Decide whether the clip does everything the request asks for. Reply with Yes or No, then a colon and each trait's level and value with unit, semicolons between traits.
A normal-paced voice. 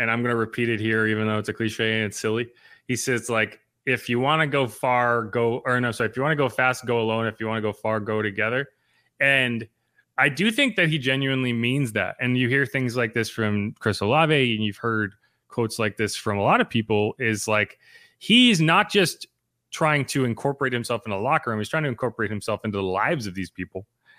No: fast, 240 wpm